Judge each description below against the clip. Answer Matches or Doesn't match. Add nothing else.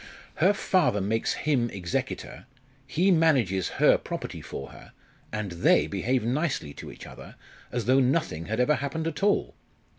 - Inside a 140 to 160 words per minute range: Matches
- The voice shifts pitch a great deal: Matches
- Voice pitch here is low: Matches